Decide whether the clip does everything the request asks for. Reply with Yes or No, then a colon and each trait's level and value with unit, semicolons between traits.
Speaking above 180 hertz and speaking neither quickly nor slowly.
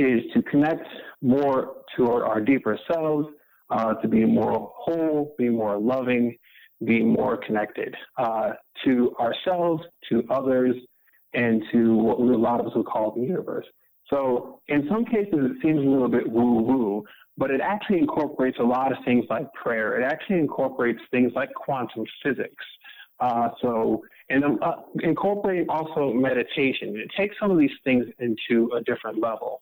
No: low, 130 Hz; average, 160 wpm